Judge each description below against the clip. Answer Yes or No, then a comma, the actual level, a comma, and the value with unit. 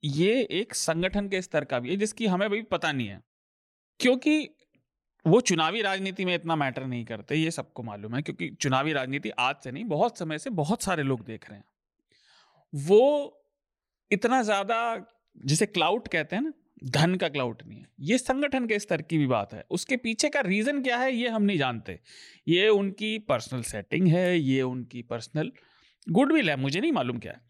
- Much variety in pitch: Yes, wide, 8.4 semitones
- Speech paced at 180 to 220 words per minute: Yes, fast, 190 wpm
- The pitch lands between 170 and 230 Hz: Yes, medium, 180 Hz